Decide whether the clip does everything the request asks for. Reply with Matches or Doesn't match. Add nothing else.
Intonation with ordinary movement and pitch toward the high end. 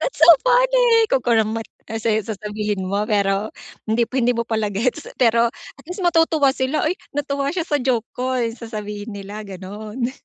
Matches